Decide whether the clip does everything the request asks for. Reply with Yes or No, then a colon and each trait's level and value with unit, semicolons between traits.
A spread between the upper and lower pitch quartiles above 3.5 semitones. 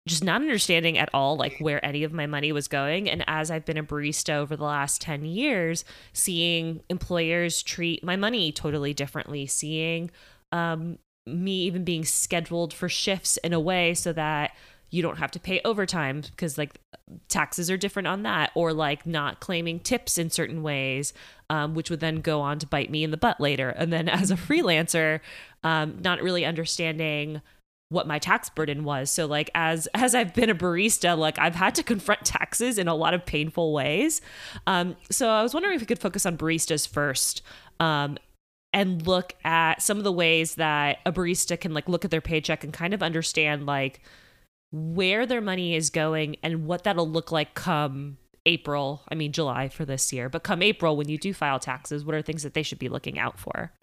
No: average, 2.9 semitones